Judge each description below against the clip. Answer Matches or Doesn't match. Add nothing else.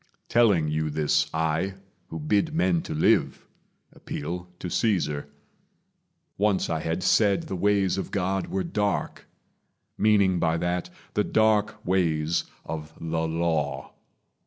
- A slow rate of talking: Matches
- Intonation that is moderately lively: Matches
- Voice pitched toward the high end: Doesn't match